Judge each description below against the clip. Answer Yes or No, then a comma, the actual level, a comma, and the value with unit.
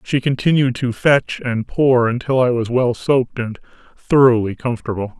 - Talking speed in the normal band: Yes, average, 160 wpm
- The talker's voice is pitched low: Yes, low, 125 Hz